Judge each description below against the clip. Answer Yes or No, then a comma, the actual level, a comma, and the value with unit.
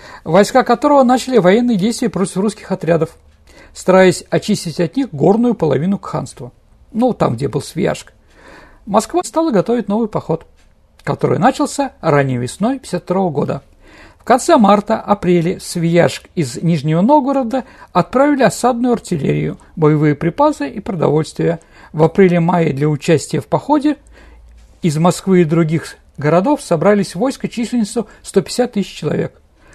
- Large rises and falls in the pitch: Yes, wide, 6.5 semitones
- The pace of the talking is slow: No, average, 130 wpm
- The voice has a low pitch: No, medium, 185 Hz